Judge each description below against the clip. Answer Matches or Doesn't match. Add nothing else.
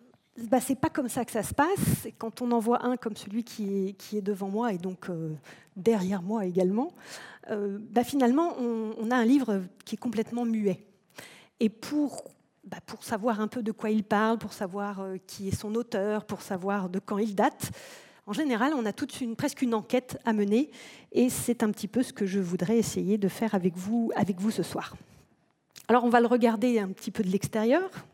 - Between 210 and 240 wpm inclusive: Matches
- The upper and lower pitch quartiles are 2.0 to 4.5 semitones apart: Matches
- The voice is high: Matches